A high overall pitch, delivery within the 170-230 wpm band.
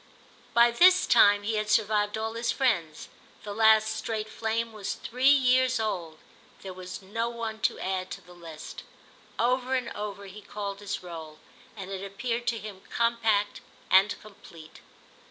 No: high, 215 Hz; average, 160 wpm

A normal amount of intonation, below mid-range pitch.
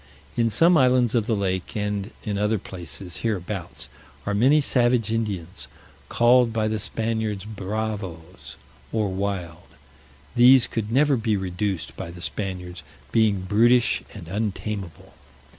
Yes: average, 3.4 semitones; low, 105 Hz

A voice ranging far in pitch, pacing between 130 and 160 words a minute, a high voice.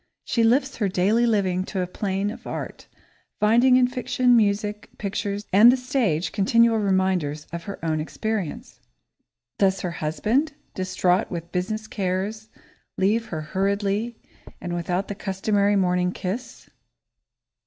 No: average, 3.3 semitones; slow, 135 wpm; high, 200 Hz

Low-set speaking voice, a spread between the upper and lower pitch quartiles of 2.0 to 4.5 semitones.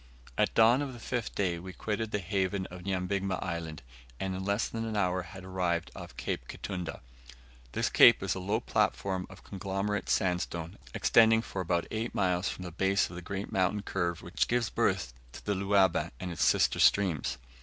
Yes: very low, 95 Hz; narrow, 2.4 semitones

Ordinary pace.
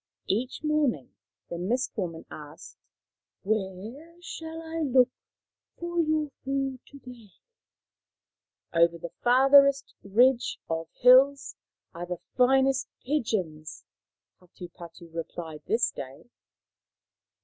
No: slow, 110 wpm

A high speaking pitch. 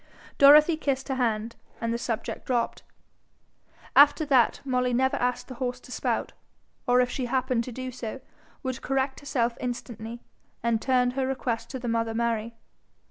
Yes: very high, 250 Hz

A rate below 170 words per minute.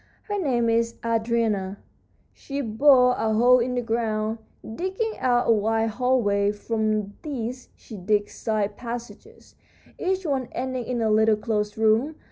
Yes: average, 145 wpm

